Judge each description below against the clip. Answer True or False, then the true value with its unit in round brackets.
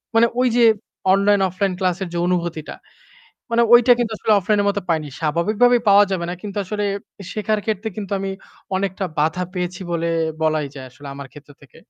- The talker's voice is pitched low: False (190 Hz)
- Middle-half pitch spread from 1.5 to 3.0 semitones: False (3.8 semitones)